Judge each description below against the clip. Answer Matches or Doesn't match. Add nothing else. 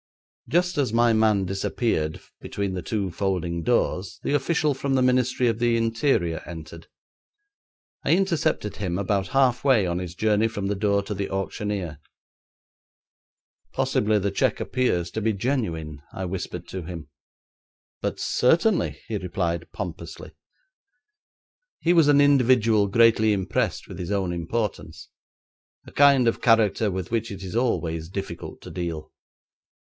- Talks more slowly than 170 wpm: Matches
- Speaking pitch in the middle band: Doesn't match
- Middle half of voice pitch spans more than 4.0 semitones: Matches